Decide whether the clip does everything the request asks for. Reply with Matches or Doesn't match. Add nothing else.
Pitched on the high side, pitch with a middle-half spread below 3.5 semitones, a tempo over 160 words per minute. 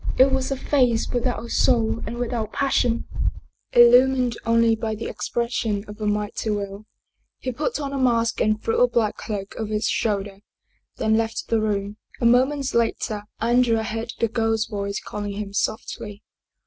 Matches